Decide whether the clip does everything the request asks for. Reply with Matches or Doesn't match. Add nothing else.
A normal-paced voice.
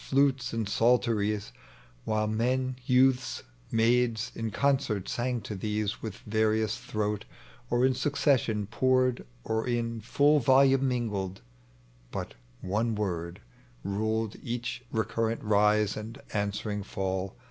Doesn't match